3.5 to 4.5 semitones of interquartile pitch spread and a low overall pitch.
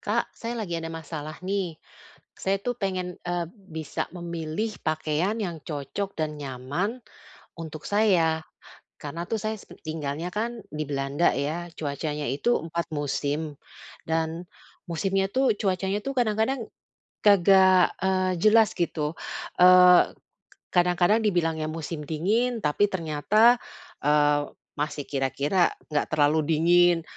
No: average, 4.2 semitones; medium, 170 Hz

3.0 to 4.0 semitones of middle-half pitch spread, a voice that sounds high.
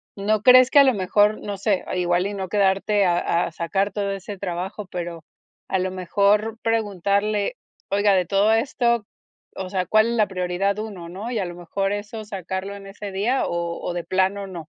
No: narrow, 2.4 semitones; high, 200 Hz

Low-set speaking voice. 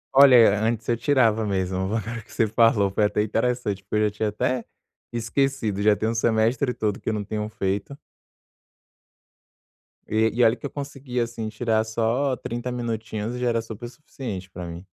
Yes: low, 110 Hz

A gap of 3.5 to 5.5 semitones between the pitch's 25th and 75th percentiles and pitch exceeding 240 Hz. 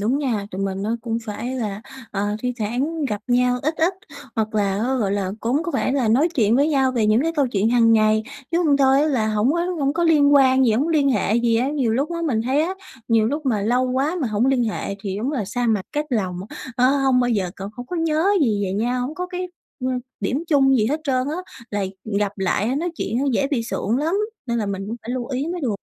Yes: average, 4.7 semitones; very high, 250 Hz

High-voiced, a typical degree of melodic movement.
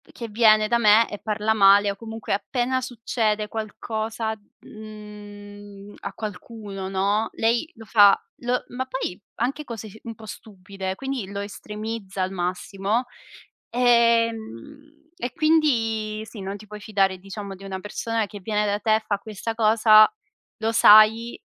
No: high, 215 Hz; narrow, 2.2 semitones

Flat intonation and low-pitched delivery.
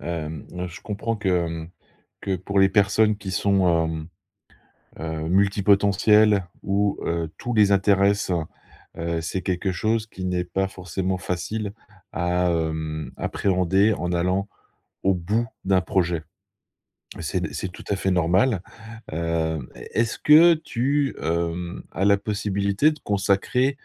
No: average, 3.2 semitones; very low, 95 Hz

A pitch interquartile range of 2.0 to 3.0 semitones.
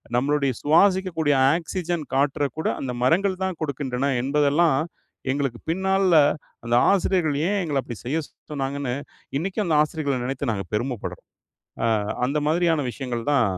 No: average, 4.3 semitones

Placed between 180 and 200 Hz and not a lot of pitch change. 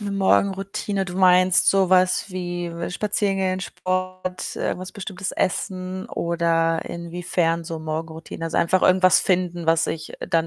Yes: medium, 185 Hz; narrow, 1.8 semitones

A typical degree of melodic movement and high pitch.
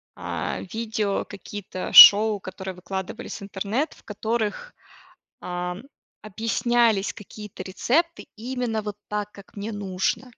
Yes: average, 3.0 semitones; high, 210 Hz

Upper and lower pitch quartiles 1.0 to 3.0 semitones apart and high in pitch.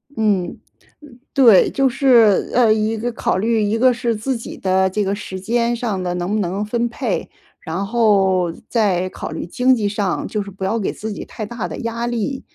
No: average, 3.6 semitones; high, 215 Hz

